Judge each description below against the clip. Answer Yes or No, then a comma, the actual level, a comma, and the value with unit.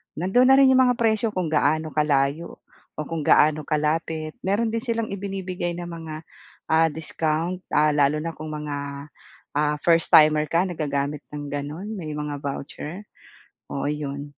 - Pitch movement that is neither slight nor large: Yes, average, 3.4 semitones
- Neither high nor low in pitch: Yes, medium, 155 Hz